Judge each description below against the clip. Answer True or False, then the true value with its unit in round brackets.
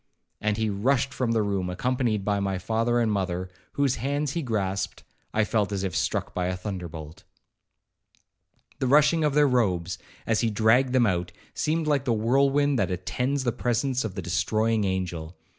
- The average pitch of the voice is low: True (110 Hz)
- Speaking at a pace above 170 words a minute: True (180 wpm)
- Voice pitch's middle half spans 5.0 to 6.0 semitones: True (5.3 semitones)